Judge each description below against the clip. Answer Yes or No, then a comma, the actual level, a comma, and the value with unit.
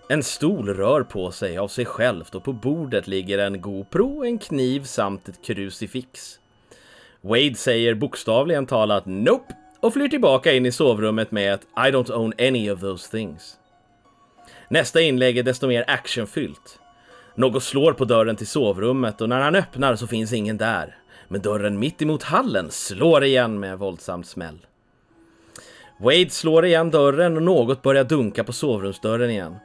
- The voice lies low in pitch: Yes, low, 125 Hz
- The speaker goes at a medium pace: Yes, average, 165 wpm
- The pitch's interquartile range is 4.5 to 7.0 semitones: Yes, average, 4.9 semitones